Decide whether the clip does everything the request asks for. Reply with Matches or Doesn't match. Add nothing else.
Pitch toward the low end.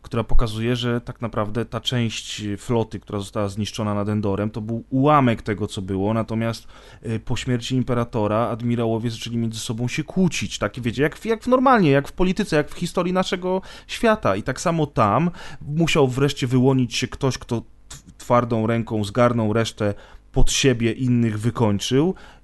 Matches